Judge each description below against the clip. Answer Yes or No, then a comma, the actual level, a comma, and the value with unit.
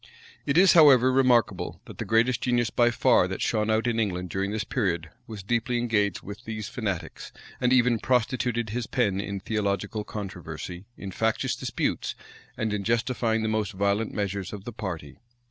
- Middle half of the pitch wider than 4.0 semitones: No, average, 3.2 semitones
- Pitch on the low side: Yes, low, 110 Hz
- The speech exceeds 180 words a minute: No, average, 175 wpm